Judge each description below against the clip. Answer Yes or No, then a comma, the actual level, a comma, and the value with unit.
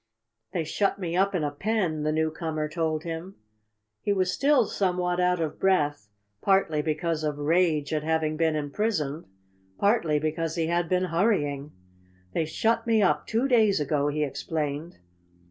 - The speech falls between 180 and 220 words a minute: No, average, 160 wpm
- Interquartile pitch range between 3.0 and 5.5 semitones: Yes, average, 3.8 semitones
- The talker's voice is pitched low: No, medium, 165 Hz